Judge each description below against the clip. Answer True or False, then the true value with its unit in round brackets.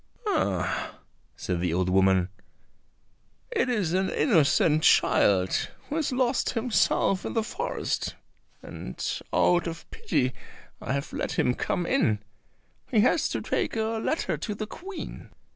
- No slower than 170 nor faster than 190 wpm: False (140 wpm)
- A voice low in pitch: False (180 Hz)